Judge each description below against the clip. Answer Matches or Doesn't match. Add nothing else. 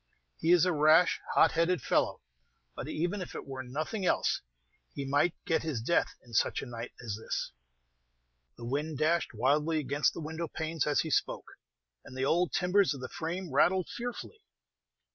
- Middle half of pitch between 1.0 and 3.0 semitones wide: Doesn't match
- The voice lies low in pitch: Doesn't match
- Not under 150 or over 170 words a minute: Doesn't match